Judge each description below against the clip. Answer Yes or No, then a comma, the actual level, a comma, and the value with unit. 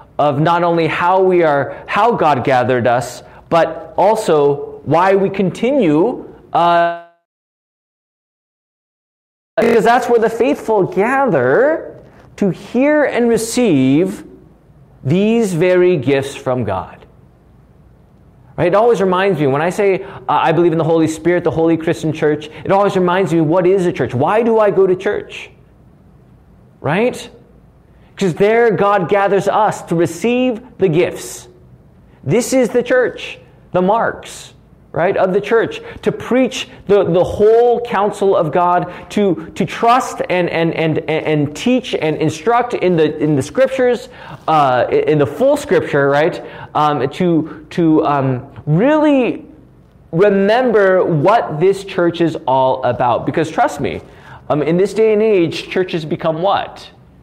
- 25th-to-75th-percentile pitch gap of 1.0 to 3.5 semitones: No, wide, 5.5 semitones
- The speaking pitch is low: No, medium, 180 Hz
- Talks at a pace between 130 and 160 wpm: Yes, average, 145 wpm